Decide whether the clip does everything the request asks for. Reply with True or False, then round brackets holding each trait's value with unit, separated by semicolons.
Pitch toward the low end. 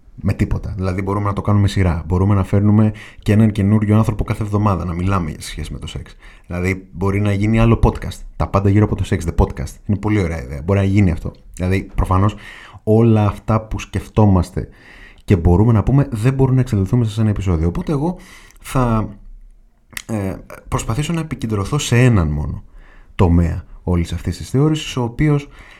True (105 Hz)